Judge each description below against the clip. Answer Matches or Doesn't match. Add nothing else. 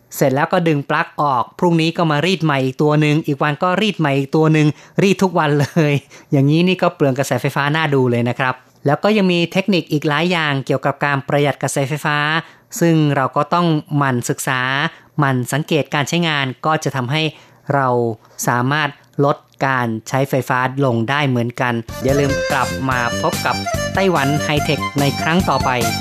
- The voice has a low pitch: Doesn't match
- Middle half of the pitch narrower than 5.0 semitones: Matches